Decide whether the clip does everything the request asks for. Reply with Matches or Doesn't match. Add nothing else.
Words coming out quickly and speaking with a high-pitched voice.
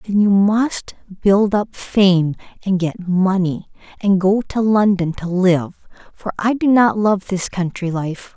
Doesn't match